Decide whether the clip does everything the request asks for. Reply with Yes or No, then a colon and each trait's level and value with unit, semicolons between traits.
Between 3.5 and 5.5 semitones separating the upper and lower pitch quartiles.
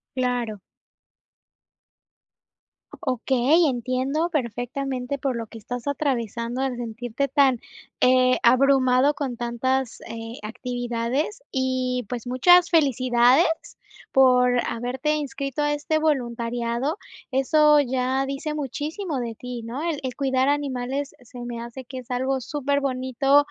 No: narrow, 2.5 semitones